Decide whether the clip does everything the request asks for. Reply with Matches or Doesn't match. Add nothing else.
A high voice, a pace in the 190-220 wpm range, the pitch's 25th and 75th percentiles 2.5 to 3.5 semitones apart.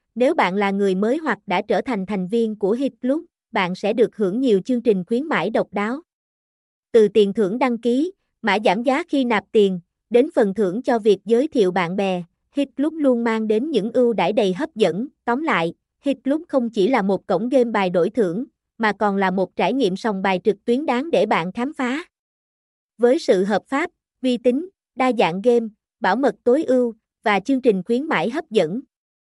Doesn't match